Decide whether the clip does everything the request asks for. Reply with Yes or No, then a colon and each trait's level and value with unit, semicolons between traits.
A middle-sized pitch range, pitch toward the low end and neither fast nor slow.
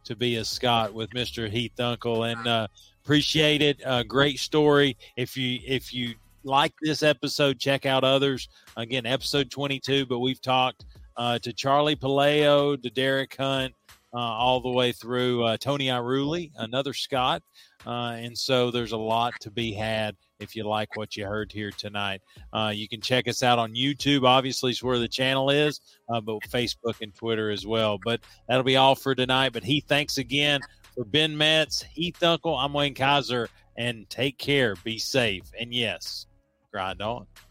Yes: average, 3.3 semitones; low, 125 Hz; average, 180 wpm